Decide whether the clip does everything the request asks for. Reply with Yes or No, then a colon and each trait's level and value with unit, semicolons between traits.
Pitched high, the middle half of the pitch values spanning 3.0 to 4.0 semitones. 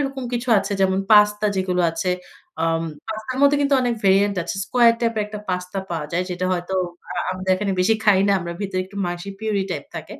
Yes: high, 195 Hz; average, 3.3 semitones